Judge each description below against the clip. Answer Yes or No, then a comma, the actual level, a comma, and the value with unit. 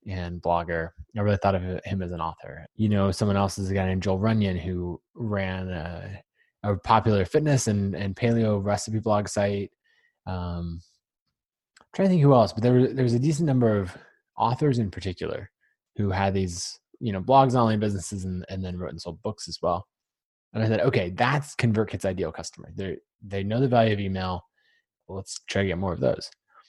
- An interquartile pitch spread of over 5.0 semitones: No, average, 3.5 semitones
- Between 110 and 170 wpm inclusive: No, fast, 205 wpm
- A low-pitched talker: Yes, low, 100 Hz